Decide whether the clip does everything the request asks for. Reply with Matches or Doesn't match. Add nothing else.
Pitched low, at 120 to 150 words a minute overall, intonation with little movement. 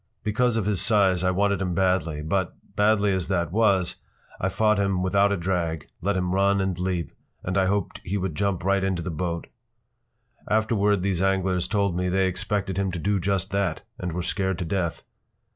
Doesn't match